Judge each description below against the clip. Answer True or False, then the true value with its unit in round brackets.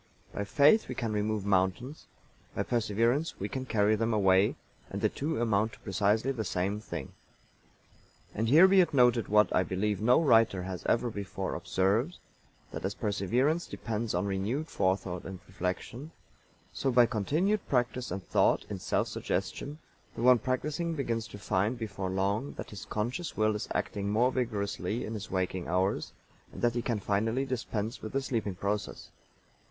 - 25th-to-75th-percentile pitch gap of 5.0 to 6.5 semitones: False (4.0 semitones)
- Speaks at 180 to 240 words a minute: False (170 wpm)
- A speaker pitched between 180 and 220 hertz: False (110 Hz)